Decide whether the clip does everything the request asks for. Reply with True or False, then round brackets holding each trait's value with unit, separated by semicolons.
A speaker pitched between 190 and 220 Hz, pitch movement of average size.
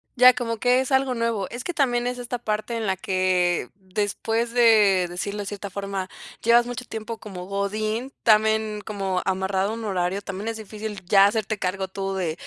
True (210 Hz; 3.2 semitones)